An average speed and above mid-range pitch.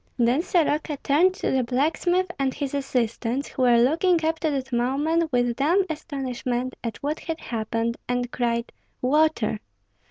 Yes: average, 155 wpm; very high, 270 Hz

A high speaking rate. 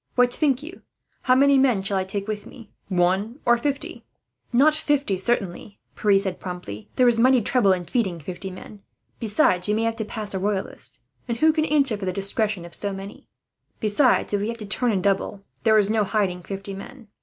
Yes: fast, 210 wpm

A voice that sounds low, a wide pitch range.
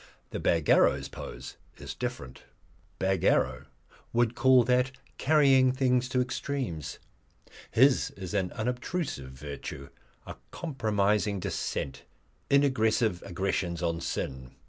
Yes: low, 110 Hz; wide, 6.8 semitones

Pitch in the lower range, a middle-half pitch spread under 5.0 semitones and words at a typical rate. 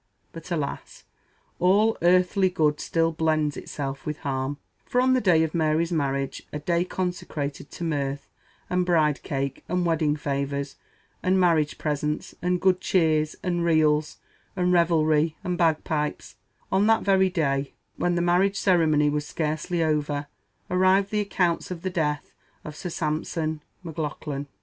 No: medium, 160 Hz; average, 3.2 semitones; average, 150 wpm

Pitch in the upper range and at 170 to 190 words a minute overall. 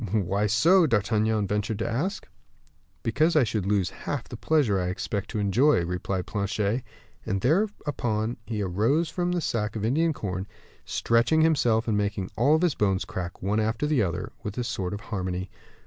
No: low, 110 Hz; average, 175 wpm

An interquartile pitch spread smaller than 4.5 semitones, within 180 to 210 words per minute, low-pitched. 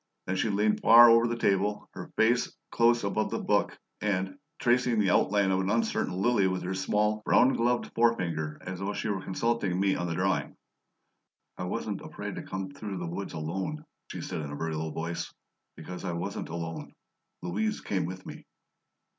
Yes: average, 3.7 semitones; average, 190 wpm; very low, 95 Hz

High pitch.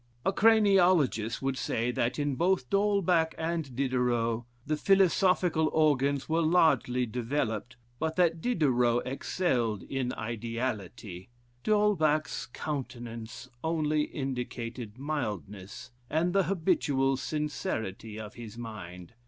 No: low, 135 Hz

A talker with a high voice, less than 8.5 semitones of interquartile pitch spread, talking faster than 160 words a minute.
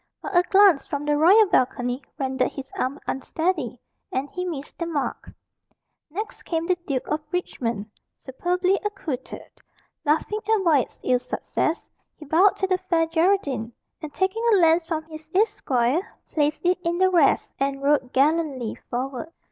No: very high, 315 Hz; average, 5.1 semitones; average, 155 wpm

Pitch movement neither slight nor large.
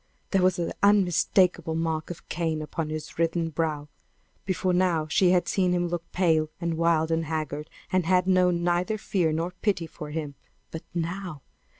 No: narrow, 2.3 semitones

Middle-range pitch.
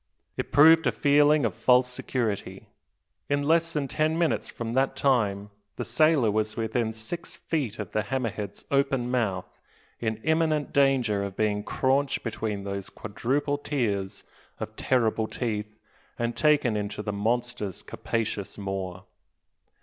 No: low, 120 Hz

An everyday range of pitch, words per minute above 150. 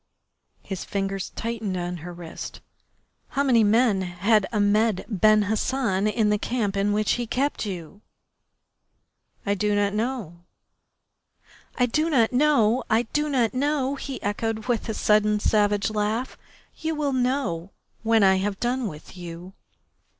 No: average, 3.8 semitones; average, 145 wpm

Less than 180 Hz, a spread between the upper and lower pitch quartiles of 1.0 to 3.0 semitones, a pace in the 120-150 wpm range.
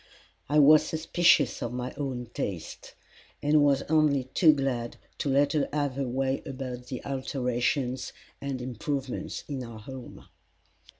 Yes: low, 135 Hz; narrow, 2.5 semitones; average, 140 wpm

